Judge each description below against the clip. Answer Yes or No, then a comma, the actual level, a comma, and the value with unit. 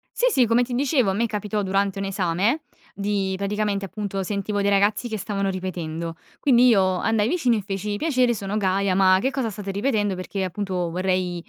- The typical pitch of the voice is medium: No, high, 200 Hz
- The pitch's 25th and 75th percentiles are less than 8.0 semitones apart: Yes, narrow, 2.6 semitones